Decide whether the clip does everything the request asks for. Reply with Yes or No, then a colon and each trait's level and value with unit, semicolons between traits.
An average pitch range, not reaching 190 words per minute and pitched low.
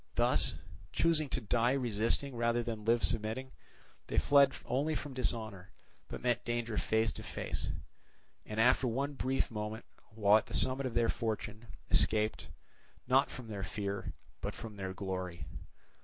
Yes: average, 3.2 semitones; average, 155 wpm; low, 115 Hz